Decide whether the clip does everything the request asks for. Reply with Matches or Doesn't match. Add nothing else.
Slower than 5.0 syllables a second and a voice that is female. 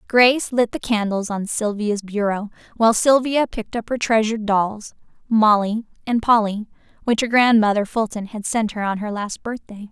Doesn't match